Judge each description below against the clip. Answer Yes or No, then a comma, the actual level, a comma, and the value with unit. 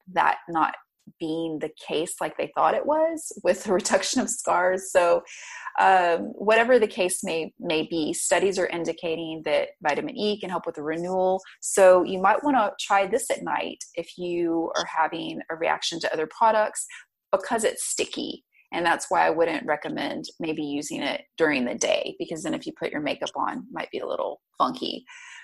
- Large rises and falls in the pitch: Yes, wide, 6.9 semitones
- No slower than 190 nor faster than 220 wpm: Yes, average, 200 wpm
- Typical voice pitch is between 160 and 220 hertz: Yes, high, 190 Hz